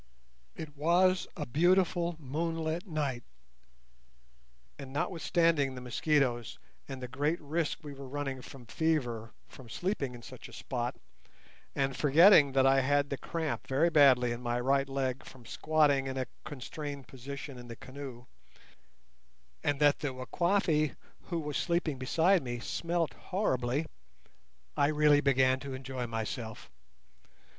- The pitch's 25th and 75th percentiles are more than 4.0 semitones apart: No, average, 3.5 semitones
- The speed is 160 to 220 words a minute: No, average, 140 wpm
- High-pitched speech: No, medium, 140 Hz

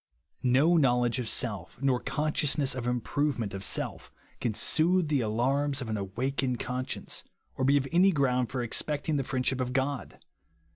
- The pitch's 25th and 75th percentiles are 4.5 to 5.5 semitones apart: No, average, 2.8 semitones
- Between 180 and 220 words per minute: No, average, 155 wpm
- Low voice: Yes, low, 130 Hz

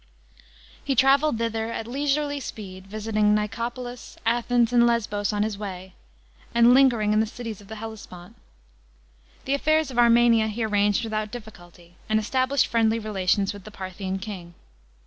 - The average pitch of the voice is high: Yes, high, 220 Hz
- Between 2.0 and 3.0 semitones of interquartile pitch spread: Yes, average, 2.7 semitones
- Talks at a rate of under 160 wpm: Yes, average, 150 wpm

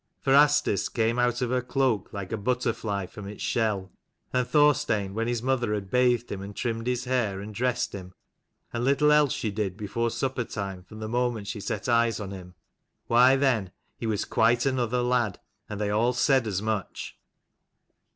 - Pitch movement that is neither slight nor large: Yes, average, 3.5 semitones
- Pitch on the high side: No, low, 115 Hz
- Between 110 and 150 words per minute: No, average, 190 wpm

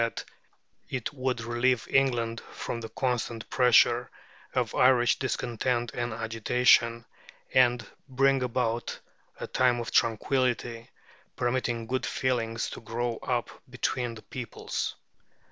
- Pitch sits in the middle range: No, low, 120 Hz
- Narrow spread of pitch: Yes, narrow, 1.6 semitones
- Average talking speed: No, slow, 115 wpm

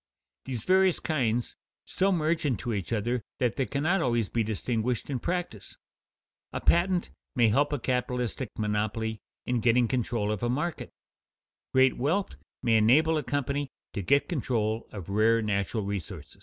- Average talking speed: Yes, average, 155 wpm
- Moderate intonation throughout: Yes, average, 4.7 semitones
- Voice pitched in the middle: No, low, 120 Hz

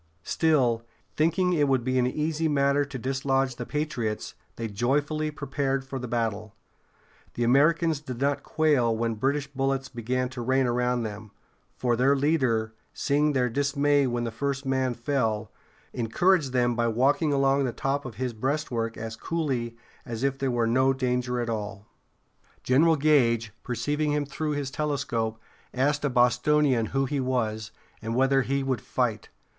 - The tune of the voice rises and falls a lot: No, average, 3.2 semitones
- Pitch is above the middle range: No, low, 130 Hz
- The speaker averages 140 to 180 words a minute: Yes, average, 160 wpm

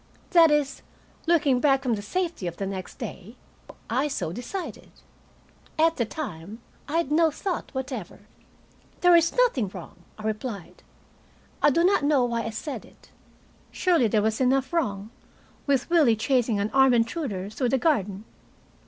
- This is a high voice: Yes, very high, 260 Hz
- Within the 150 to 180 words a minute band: Yes, average, 160 wpm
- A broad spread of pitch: Yes, wide, 6.5 semitones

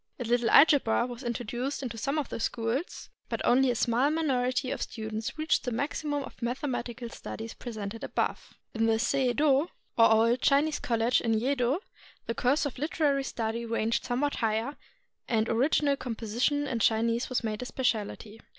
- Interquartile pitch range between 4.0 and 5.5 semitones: No, average, 3.5 semitones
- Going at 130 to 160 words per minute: No, average, 170 wpm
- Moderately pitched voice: No, high, 245 Hz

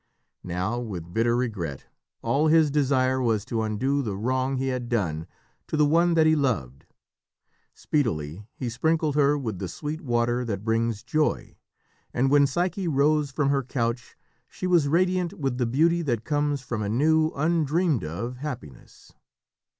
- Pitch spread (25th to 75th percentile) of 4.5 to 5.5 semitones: Yes, average, 4.8 semitones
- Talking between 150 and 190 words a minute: Yes, average, 160 wpm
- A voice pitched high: No, low, 130 Hz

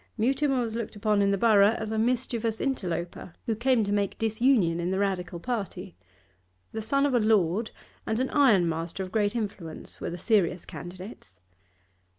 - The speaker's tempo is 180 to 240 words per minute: No, average, 170 wpm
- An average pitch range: Yes, average, 4.2 semitones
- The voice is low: No, high, 210 Hz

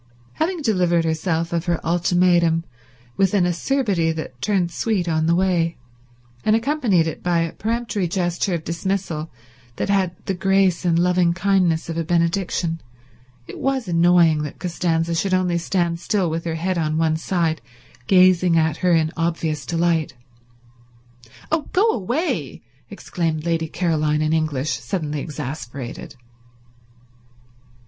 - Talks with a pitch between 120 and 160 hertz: No, medium, 170 Hz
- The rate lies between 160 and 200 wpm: No, average, 140 wpm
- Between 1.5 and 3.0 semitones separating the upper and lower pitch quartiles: Yes, narrow, 2.5 semitones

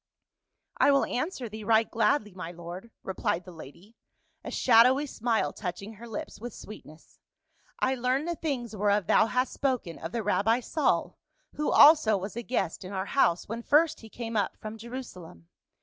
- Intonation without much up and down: No, average, 4.6 semitones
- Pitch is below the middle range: No, high, 225 Hz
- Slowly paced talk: No, average, 185 wpm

